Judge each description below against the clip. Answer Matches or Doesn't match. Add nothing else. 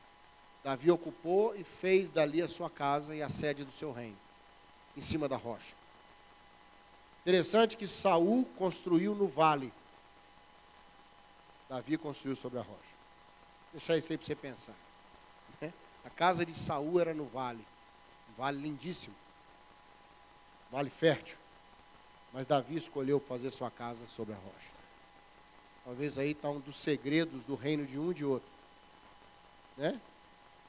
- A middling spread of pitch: Matches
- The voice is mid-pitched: Matches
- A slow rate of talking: Doesn't match